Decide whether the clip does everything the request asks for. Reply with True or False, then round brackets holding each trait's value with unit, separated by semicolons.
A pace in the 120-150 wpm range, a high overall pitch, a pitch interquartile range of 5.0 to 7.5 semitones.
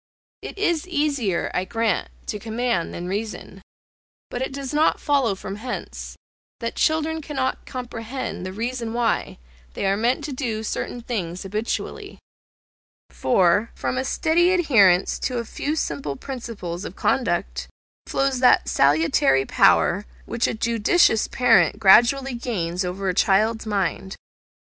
True (140 wpm; 230 Hz; 5.4 semitones)